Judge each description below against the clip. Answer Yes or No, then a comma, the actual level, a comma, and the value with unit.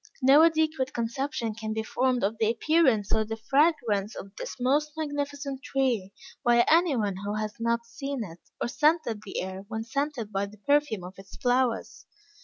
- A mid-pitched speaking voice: No, high, 235 Hz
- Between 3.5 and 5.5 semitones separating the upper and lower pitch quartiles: Yes, average, 4.9 semitones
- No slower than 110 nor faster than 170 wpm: No, average, 180 wpm